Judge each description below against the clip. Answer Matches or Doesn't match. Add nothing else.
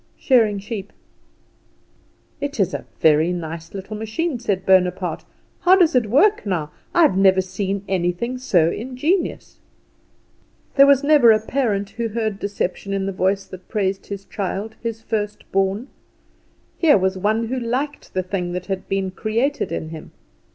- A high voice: Matches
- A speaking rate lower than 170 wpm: Matches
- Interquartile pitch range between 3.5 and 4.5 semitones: Matches